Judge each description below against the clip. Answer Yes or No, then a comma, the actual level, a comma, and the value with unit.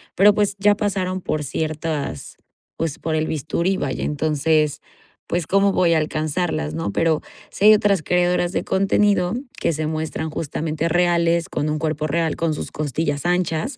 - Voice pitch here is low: No, medium, 165 Hz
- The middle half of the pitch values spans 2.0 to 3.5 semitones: Yes, average, 2.8 semitones